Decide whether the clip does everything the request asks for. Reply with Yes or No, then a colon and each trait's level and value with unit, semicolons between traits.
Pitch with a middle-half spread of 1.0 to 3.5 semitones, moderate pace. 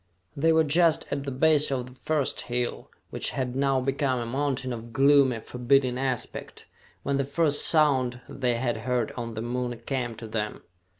Yes: narrow, 2.5 semitones; average, 180 wpm